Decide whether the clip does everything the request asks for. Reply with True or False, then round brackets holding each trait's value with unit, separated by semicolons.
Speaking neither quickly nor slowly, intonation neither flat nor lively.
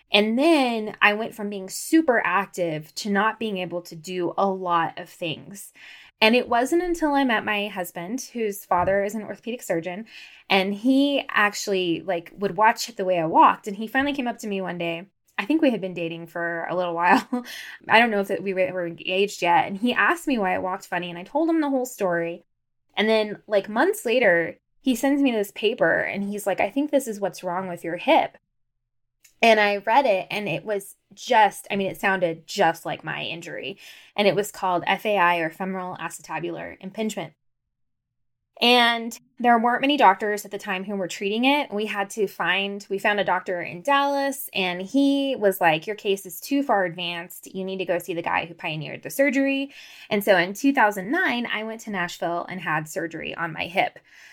False (210 wpm; 4.9 semitones)